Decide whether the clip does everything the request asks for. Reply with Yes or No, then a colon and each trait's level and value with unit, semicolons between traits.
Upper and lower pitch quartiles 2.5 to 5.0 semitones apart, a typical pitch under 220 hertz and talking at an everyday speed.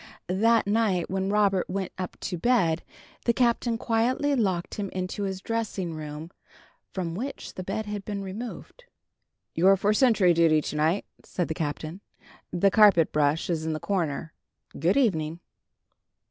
Yes: average, 4.4 semitones; high, 190 Hz; average, 155 wpm